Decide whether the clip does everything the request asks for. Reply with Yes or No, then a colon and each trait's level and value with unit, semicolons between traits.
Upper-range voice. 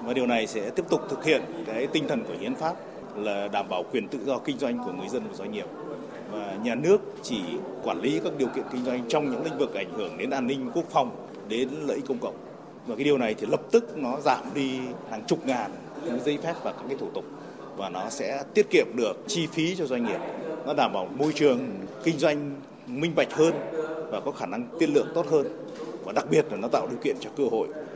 No: medium, 150 Hz